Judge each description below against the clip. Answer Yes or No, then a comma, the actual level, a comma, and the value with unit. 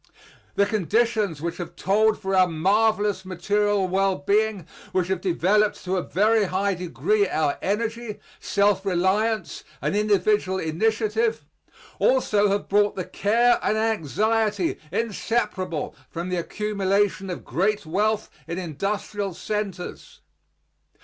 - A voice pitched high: Yes, high, 200 Hz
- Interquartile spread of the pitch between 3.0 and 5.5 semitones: No, narrow, 2.6 semitones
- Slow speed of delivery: Yes, slow, 125 wpm